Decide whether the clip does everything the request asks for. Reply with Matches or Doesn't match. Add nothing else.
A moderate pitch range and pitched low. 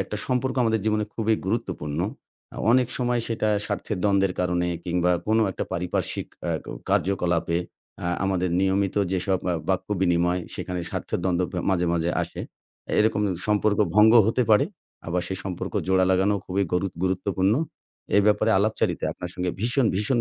Matches